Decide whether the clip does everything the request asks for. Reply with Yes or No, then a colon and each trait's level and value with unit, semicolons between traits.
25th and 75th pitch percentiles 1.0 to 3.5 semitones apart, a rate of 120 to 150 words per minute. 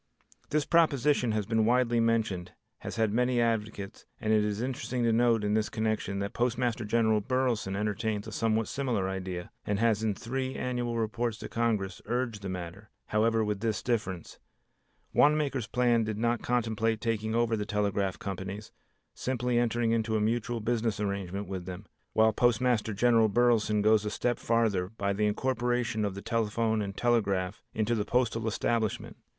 No: narrow, 2.4 semitones; average, 165 wpm